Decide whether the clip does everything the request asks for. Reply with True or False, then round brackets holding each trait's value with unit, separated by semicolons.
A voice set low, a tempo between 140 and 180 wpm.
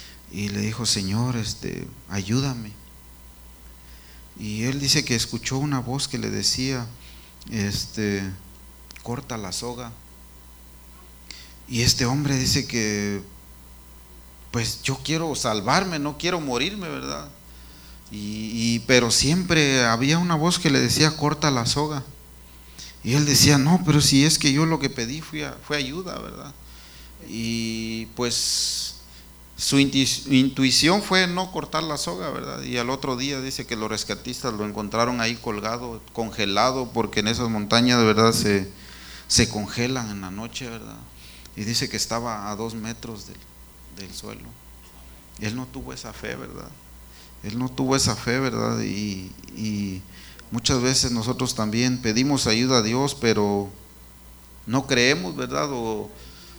True (115 Hz; 145 wpm)